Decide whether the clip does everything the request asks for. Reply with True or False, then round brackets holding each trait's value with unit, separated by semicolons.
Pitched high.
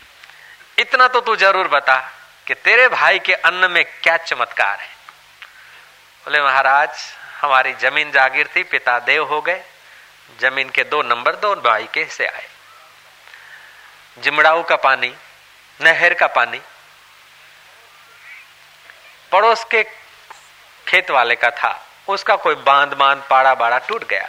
False (150 Hz)